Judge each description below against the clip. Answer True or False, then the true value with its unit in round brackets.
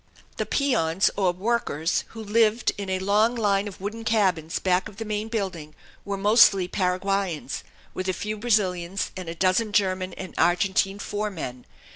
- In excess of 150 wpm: True (160 wpm)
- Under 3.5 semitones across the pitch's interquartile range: True (2.6 semitones)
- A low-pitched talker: False (195 Hz)